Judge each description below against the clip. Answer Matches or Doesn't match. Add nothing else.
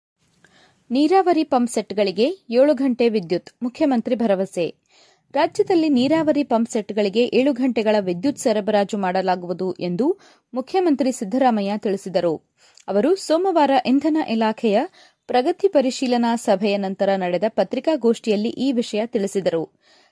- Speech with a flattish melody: Doesn't match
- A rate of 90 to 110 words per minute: Matches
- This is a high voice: Matches